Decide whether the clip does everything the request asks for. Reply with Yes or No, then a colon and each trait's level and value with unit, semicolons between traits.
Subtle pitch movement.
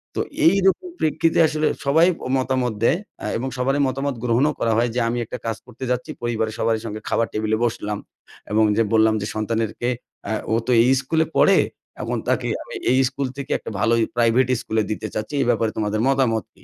No: average, 3.4 semitones